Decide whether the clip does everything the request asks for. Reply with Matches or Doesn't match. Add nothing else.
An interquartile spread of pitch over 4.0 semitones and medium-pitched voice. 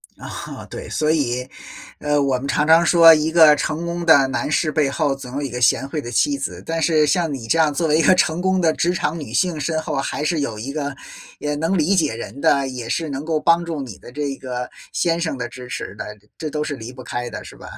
Doesn't match